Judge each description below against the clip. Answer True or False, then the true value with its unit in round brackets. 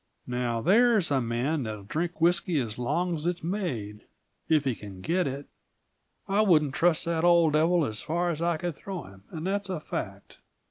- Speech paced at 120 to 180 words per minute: False (190 wpm)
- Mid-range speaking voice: True (160 Hz)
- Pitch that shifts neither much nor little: False (5.9 semitones)